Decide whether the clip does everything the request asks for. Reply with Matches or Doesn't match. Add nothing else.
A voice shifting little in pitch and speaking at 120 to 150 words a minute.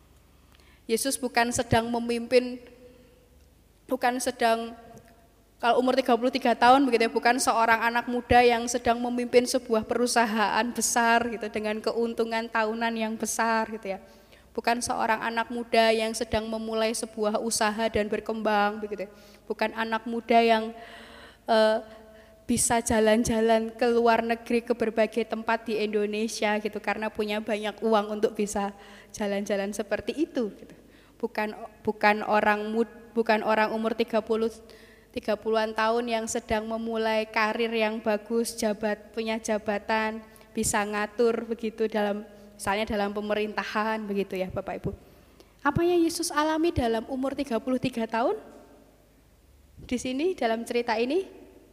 Matches